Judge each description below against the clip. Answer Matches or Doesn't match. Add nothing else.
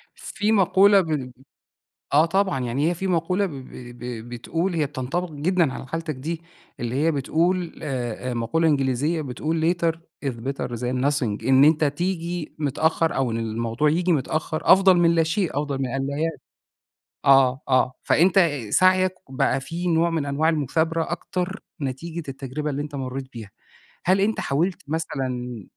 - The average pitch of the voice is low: Doesn't match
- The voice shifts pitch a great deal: Doesn't match